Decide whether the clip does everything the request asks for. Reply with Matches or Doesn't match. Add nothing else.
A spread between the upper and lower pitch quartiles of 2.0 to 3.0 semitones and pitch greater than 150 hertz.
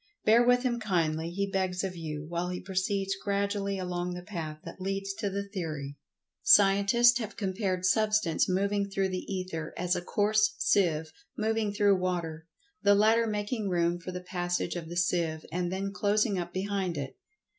Matches